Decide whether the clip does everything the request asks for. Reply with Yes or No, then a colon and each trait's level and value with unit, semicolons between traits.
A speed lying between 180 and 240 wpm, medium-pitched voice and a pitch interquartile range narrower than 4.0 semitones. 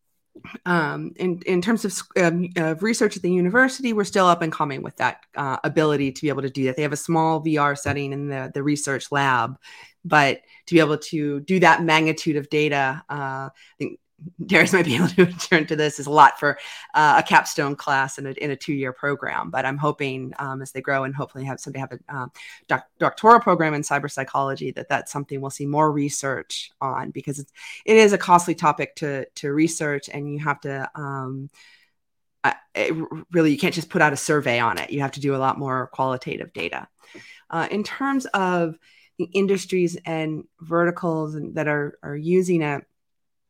Yes: fast, 205 wpm; medium, 150 Hz; average, 3.6 semitones